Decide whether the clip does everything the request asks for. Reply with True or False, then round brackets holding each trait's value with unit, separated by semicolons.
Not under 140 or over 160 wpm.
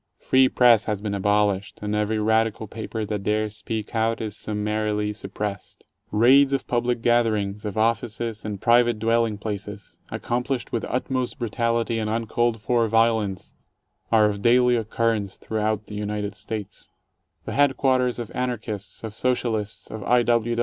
True (150 wpm)